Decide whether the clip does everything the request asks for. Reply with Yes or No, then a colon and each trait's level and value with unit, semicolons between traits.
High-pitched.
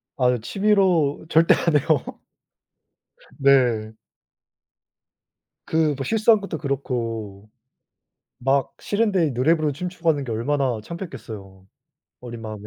No: medium, 140 Hz